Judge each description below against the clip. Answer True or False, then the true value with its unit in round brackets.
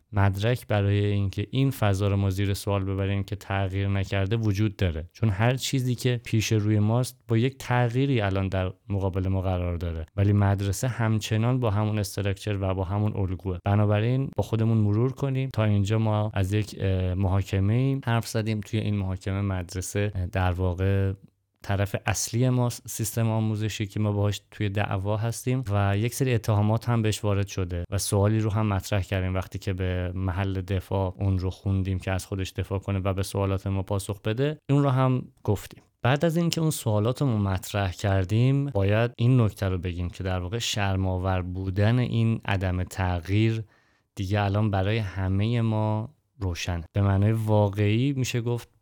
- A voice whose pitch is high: False (105 Hz)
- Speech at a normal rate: False (175 wpm)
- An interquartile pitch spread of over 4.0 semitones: False (2.7 semitones)